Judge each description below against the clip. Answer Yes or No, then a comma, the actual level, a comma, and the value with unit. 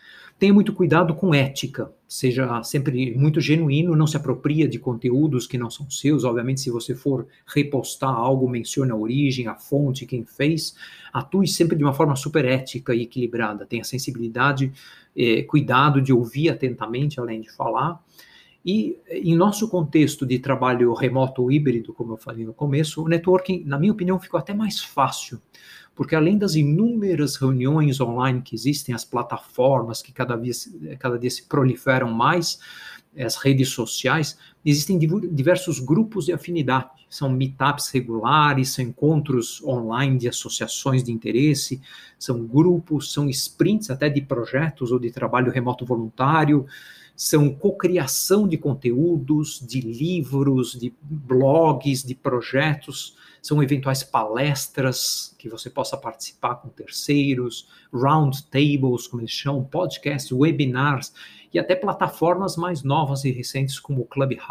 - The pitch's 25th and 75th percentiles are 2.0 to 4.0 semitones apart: Yes, average, 3.6 semitones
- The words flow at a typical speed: Yes, average, 145 wpm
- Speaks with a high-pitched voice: No, medium, 140 Hz